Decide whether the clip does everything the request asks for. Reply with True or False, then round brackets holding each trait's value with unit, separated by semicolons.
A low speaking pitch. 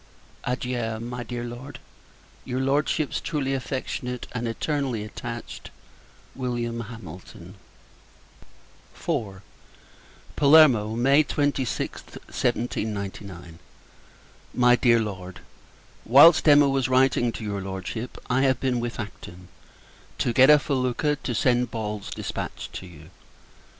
True (120 Hz)